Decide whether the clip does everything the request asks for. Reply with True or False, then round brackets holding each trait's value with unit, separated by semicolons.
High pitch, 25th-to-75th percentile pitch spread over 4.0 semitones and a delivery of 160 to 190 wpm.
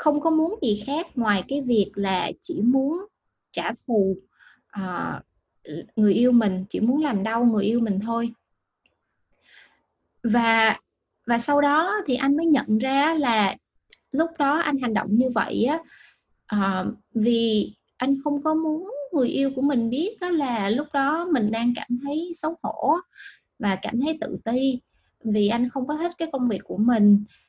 True (245 Hz; 5.2 semitones; 170 wpm)